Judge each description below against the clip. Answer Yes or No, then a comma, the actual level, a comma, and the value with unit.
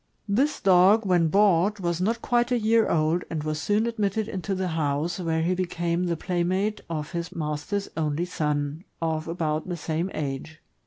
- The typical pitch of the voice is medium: Yes, medium, 175 Hz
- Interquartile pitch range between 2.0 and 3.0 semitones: No, average, 3.9 semitones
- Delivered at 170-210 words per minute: Yes, average, 175 wpm